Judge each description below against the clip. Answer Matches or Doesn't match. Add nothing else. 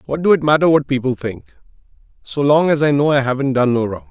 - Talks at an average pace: Doesn't match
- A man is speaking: Matches